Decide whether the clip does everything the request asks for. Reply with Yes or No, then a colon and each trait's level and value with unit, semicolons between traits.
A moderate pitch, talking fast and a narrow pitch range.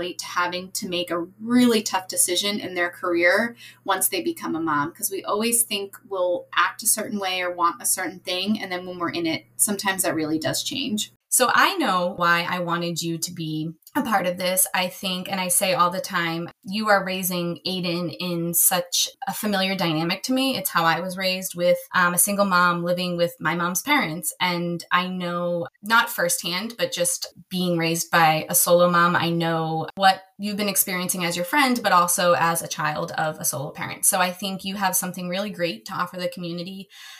Yes: medium, 180 Hz; fast, 210 wpm; narrow, 2.3 semitones